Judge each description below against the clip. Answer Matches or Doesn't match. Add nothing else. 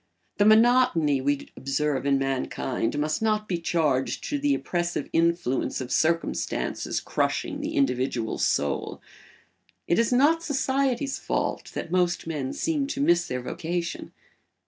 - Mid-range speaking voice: Matches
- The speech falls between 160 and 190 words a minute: Doesn't match